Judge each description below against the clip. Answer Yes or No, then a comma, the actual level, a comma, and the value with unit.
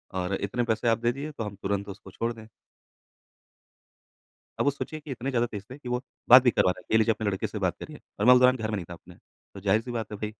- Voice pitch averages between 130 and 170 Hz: No, low, 110 Hz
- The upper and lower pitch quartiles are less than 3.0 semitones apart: No, average, 3.5 semitones